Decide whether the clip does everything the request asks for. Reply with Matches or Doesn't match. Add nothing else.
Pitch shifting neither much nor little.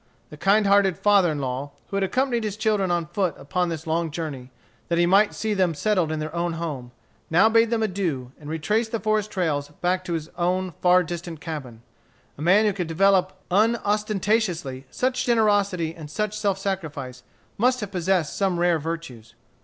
Matches